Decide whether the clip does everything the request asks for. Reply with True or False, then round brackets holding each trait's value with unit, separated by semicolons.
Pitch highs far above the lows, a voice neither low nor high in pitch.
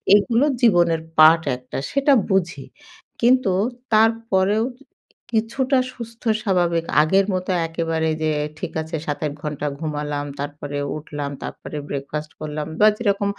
True (6.1 semitones; 170 Hz)